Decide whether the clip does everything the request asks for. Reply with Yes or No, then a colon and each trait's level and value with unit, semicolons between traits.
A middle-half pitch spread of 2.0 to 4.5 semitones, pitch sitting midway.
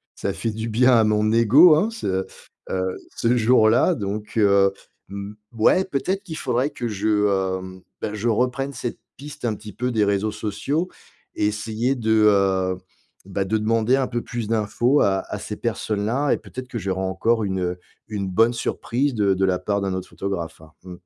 No: average, 3.8 semitones; low, 110 Hz